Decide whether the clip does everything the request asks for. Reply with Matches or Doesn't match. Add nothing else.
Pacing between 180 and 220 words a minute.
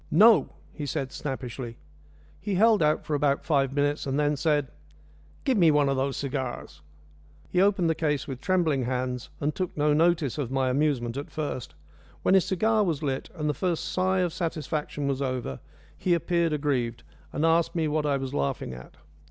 Matches